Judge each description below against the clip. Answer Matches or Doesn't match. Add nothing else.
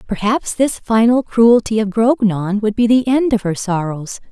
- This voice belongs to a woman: Matches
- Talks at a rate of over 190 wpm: Doesn't match